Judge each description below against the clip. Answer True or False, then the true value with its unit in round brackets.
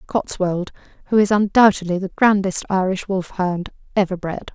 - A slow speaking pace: True (130 wpm)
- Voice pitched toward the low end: False (190 Hz)